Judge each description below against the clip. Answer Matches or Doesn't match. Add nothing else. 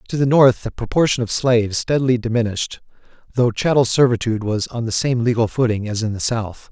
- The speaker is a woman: Doesn't match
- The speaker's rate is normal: Matches